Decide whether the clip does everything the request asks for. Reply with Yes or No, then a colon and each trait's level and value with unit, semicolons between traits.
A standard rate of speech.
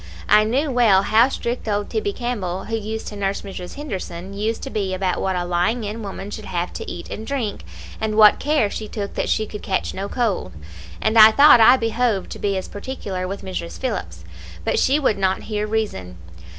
No: fast, 210 wpm